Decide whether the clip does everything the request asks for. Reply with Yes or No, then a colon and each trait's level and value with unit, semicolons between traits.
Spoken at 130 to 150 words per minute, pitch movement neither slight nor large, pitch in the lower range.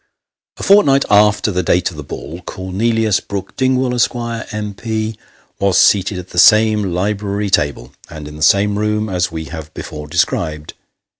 No: average, 160 wpm; average, 3.8 semitones; low, 100 Hz